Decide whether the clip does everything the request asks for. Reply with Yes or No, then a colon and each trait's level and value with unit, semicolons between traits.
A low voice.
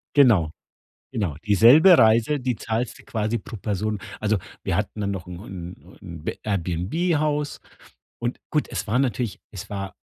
Yes: low, 110 Hz